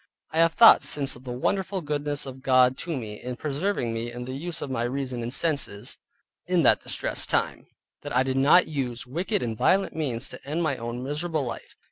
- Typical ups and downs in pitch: Yes, average, 4.3 semitones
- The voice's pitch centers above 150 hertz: No, low, 135 Hz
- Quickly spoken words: Yes, fast, 210 wpm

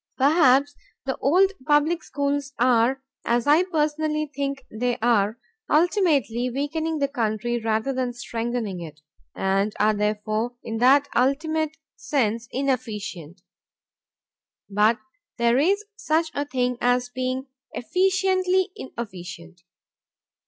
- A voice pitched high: Yes, very high, 255 Hz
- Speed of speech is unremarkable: No, slow, 110 wpm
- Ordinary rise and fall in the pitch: Yes, average, 4.9 semitones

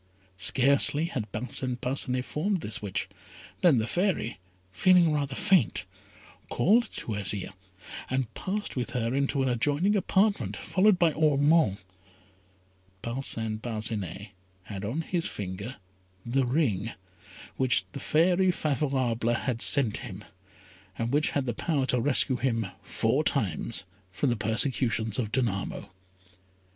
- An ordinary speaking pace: No, slow, 130 wpm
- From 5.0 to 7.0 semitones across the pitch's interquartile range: Yes, average, 5.3 semitones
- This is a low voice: Yes, low, 130 Hz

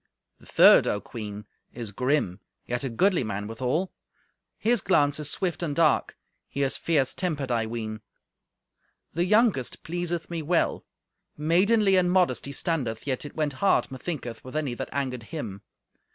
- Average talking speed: Yes, average, 160 wpm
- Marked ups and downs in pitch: Yes, wide, 6.4 semitones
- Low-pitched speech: No, medium, 145 Hz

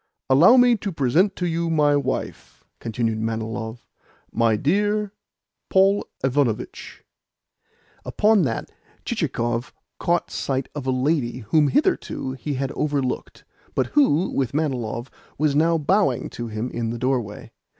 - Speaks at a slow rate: Yes, slow, 130 wpm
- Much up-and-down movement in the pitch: Yes, wide, 6.1 semitones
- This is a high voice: No, medium, 140 Hz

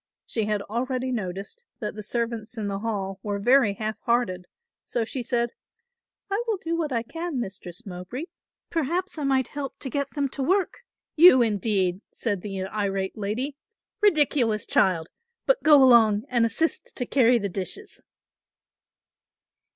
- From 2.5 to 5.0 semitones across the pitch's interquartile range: No, wide, 5.5 semitones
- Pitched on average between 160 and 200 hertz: No, high, 235 Hz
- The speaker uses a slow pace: No, average, 155 wpm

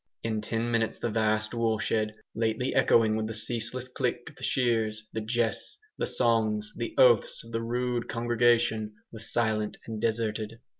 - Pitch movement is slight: Yes, narrow, 1.5 semitones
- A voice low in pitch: Yes, low, 115 Hz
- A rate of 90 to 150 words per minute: No, average, 160 wpm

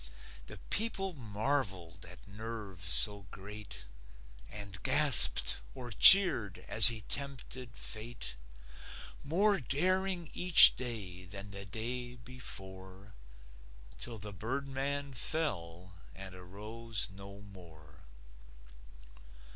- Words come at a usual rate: No, slow, 95 wpm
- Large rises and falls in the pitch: Yes, wide, 6.0 semitones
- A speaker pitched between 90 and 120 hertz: Yes, low, 110 Hz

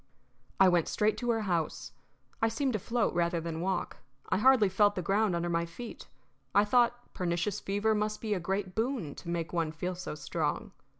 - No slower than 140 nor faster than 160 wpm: No, average, 195 wpm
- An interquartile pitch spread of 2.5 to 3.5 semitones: No, average, 4.2 semitones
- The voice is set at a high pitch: Yes, high, 195 Hz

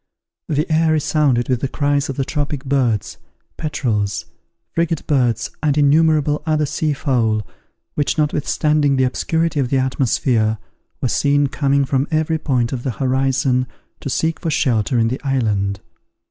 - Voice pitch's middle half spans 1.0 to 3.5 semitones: Yes, average, 3.2 semitones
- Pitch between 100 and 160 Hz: Yes, medium, 140 Hz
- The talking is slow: No, average, 150 wpm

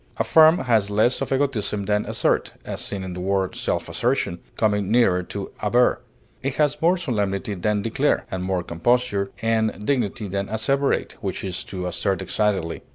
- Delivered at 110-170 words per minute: Yes, average, 165 wpm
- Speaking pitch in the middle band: No, low, 105 Hz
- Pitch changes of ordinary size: Yes, average, 4.4 semitones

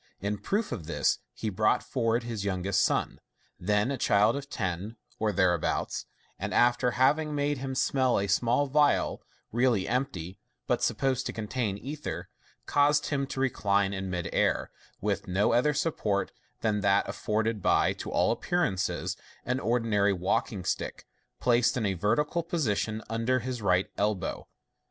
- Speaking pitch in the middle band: No, low, 115 Hz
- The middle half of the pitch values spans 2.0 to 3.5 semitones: No, average, 4.8 semitones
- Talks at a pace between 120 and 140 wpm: No, average, 160 wpm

